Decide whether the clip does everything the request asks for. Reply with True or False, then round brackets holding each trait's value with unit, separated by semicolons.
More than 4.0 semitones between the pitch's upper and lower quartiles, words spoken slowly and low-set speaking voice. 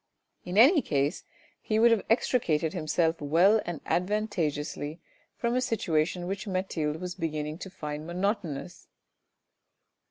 False (5.3 semitones; 125 wpm; 175 Hz)